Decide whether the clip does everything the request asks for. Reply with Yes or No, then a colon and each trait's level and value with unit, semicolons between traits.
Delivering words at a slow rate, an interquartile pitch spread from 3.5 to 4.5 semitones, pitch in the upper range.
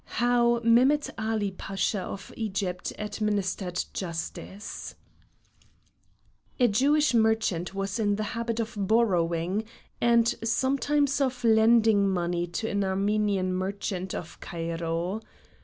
Yes: slow, 105 wpm; average, 3.8 semitones; high, 210 Hz